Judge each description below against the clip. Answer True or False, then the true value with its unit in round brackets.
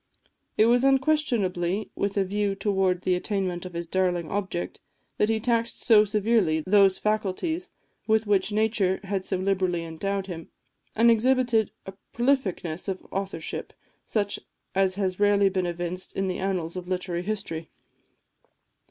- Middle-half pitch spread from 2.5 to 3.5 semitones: True (2.9 semitones)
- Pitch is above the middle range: True (195 Hz)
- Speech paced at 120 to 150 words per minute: True (145 wpm)